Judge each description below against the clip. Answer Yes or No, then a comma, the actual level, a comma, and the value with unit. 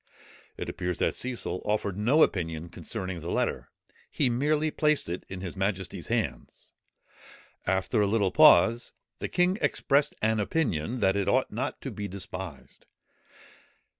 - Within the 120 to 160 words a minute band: Yes, average, 145 wpm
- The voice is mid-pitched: No, low, 100 Hz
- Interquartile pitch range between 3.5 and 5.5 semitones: Yes, average, 5.2 semitones